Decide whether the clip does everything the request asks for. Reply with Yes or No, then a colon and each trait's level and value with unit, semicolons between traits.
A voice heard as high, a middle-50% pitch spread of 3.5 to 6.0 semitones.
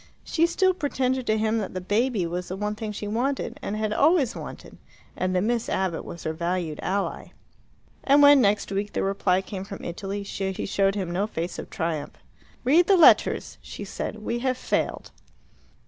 Yes: high, 205 Hz; average, 5.1 semitones